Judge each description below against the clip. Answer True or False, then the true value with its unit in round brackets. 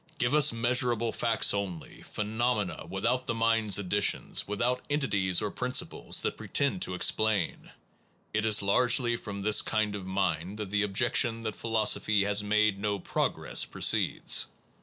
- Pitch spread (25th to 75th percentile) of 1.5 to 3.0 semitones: True (2.7 semitones)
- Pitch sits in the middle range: False (105 Hz)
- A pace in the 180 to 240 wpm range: False (155 wpm)